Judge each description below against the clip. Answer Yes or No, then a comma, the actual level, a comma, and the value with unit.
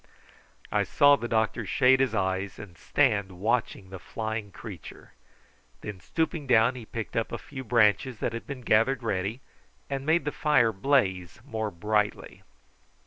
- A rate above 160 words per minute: No, average, 155 wpm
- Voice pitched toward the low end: Yes, low, 115 Hz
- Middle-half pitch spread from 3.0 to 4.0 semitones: No, average, 4.6 semitones